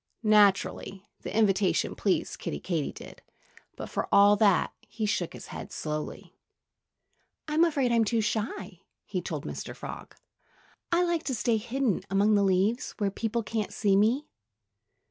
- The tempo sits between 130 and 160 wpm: Yes, average, 145 wpm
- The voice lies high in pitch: Yes, high, 210 Hz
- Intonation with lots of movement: No, average, 3.1 semitones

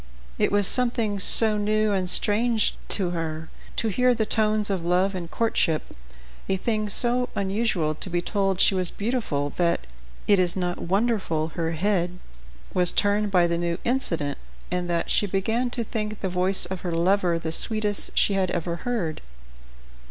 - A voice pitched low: No, high, 195 Hz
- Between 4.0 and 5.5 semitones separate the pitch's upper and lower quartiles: No, average, 3.6 semitones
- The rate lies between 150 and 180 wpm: Yes, average, 170 wpm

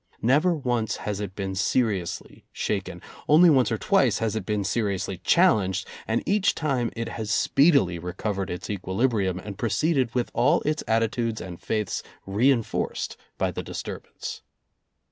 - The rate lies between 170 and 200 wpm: No, average, 145 wpm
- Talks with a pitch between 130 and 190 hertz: No, low, 110 Hz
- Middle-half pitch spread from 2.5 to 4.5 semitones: No, average, 5.1 semitones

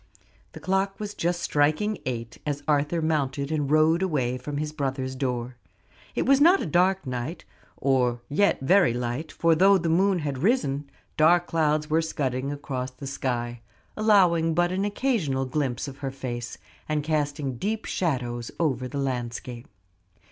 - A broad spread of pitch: No, average, 5.0 semitones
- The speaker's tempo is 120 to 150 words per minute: No, average, 160 wpm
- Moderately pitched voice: Yes, medium, 150 Hz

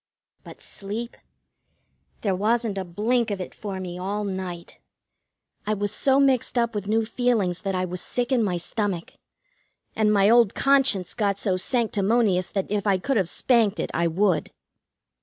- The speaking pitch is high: Yes, high, 205 Hz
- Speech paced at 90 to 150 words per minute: No, average, 170 wpm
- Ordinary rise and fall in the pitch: Yes, average, 3.7 semitones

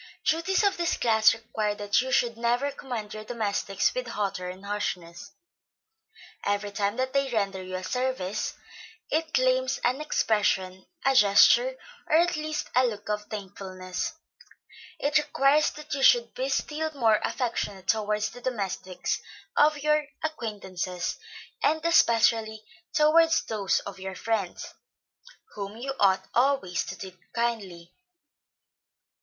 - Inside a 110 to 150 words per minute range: Yes, slow, 135 wpm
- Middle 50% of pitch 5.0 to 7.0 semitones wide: Yes, wide, 5.6 semitones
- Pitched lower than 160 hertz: No, high, 225 Hz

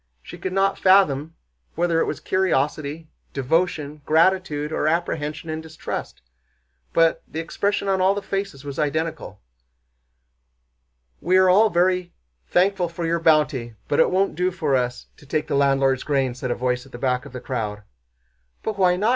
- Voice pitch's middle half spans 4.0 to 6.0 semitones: Yes, average, 5.1 semitones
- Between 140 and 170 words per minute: Yes, average, 165 wpm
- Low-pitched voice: No, medium, 155 Hz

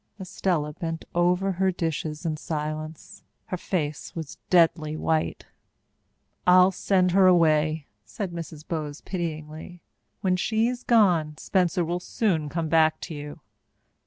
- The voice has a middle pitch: Yes, medium, 165 Hz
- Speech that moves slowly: Yes, slow, 130 wpm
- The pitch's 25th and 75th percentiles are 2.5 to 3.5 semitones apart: Yes, average, 2.8 semitones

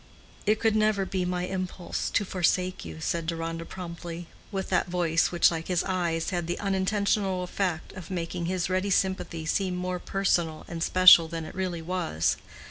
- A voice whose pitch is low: No, medium, 180 Hz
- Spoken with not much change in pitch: Yes, narrow, 2.0 semitones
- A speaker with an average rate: Yes, average, 175 wpm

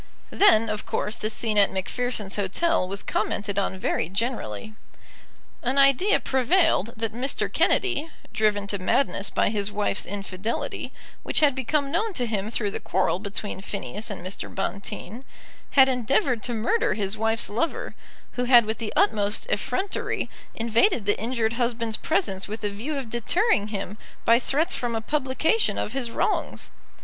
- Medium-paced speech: Yes, average, 160 wpm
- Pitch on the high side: Yes, high, 225 Hz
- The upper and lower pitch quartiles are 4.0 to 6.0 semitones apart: Yes, average, 4.4 semitones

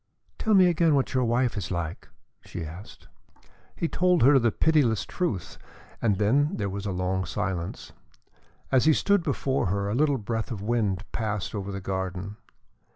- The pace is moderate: Yes, average, 170 wpm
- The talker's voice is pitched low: Yes, low, 110 Hz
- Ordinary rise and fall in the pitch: No, wide, 6.5 semitones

